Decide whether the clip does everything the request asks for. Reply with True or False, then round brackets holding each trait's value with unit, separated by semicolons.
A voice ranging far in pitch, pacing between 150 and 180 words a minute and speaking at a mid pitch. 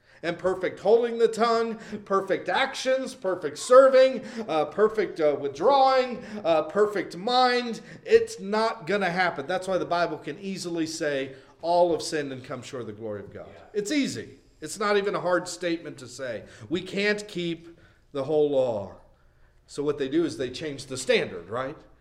True (7.3 semitones; 175 wpm; 175 Hz)